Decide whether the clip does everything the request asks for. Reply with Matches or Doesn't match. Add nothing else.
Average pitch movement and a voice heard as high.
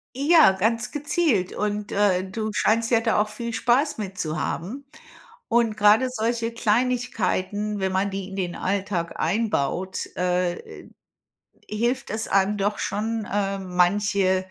Matches